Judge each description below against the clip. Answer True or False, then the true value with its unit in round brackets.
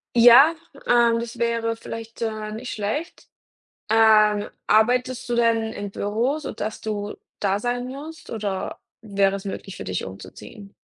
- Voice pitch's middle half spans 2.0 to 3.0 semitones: True (2.6 semitones)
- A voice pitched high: True (225 Hz)